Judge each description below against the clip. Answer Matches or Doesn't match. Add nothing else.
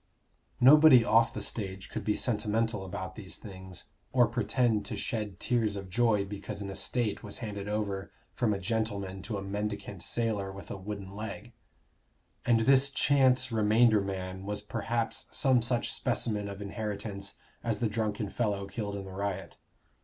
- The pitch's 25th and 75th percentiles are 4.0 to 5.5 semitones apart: Doesn't match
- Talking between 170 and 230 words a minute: Doesn't match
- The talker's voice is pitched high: Doesn't match